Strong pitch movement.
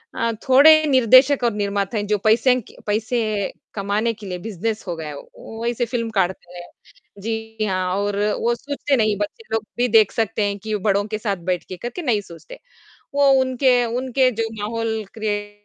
No: average, 2.9 semitones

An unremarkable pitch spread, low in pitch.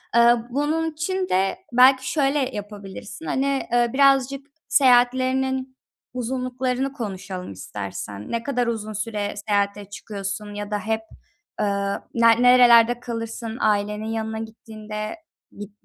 No: average, 3.9 semitones; high, 230 Hz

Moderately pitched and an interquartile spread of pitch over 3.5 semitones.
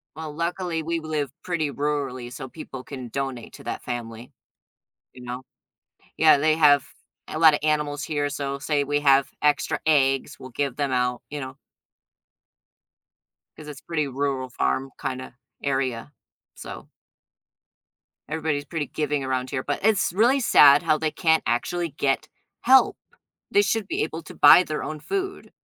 No: medium, 145 Hz; average, 2.9 semitones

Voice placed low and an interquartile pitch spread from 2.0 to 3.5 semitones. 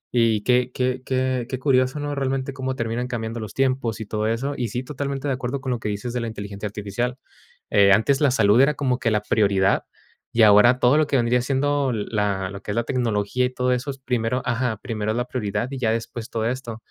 Yes: low, 125 Hz; average, 3.0 semitones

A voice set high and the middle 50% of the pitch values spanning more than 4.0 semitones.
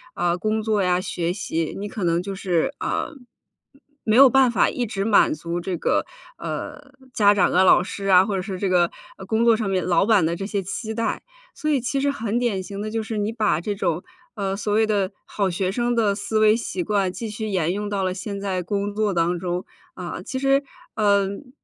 No: high, 200 Hz; average, 3.1 semitones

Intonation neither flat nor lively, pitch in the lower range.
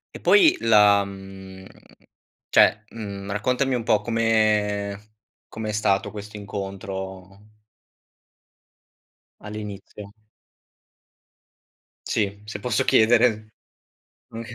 No: narrow, 1.9 semitones; low, 105 Hz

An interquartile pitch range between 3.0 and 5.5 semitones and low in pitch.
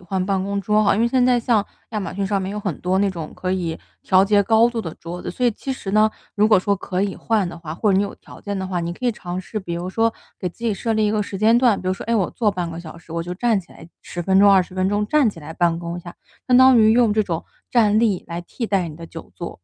No: average, 3.5 semitones; high, 195 Hz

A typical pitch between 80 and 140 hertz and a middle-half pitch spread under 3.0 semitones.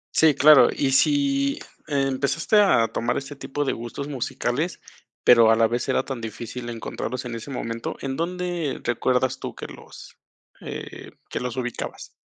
No: low, 135 Hz; average, 4.1 semitones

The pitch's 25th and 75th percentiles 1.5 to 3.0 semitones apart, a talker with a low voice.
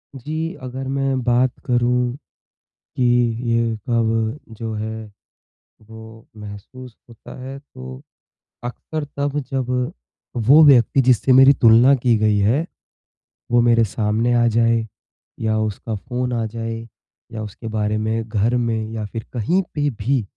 Yes: narrow, 2.6 semitones; low, 115 Hz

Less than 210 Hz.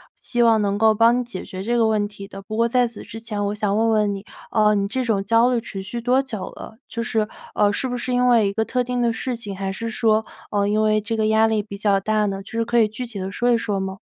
No: high, 220 Hz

